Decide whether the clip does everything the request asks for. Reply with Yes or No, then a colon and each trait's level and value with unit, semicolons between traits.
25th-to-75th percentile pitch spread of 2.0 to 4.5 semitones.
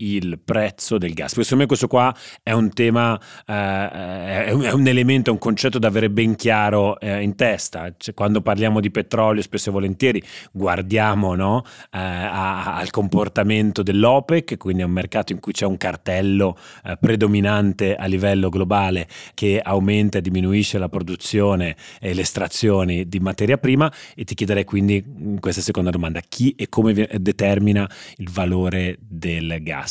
Yes: narrow, 2.5 semitones